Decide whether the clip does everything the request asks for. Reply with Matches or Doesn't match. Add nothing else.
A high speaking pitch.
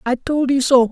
Matches